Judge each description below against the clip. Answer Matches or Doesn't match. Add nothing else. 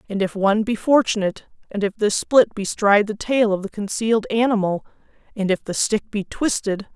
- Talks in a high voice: Matches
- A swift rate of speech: Doesn't match